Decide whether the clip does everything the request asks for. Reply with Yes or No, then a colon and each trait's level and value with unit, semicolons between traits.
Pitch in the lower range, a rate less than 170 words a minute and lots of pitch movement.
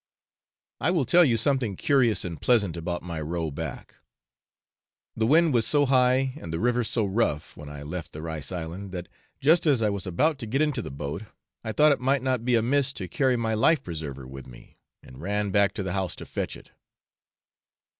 No: low, 110 Hz; fast, 205 wpm; wide, 7.8 semitones